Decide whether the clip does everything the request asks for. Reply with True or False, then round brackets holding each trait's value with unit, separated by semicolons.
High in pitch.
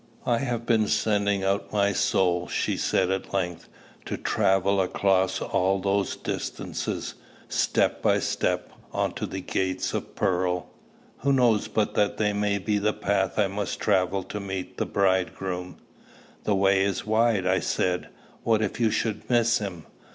False (100 Hz)